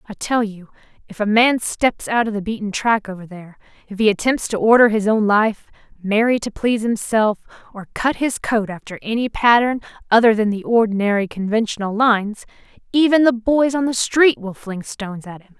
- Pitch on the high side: Yes, high, 220 Hz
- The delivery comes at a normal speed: Yes, average, 185 wpm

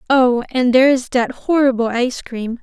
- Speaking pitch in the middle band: No, very high, 250 Hz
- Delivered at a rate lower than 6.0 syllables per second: Yes, 5.2 syllables/s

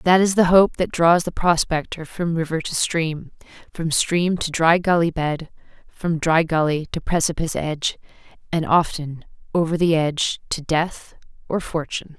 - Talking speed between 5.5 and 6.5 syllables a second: No, 4.6 syllables/s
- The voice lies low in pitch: No, medium, 165 Hz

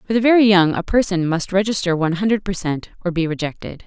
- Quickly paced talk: Yes, fast, 215 wpm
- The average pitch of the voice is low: No, medium, 185 Hz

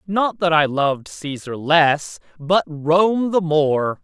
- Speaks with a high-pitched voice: No, medium, 160 Hz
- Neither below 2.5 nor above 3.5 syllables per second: Yes, 3.3 syllables/s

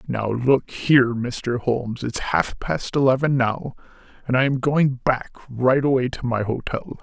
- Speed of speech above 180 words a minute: No, average, 170 wpm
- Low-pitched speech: Yes, low, 125 Hz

